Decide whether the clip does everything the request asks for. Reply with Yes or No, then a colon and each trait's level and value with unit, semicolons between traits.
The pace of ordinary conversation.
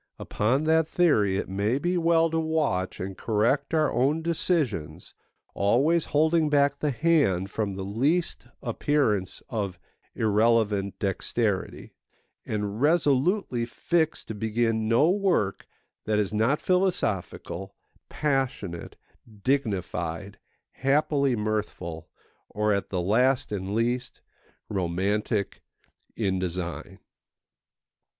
No: slow, 105 wpm